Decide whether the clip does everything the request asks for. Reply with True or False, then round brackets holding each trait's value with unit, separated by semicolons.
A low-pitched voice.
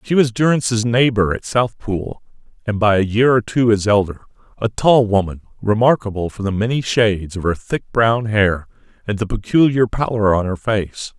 True (110 Hz)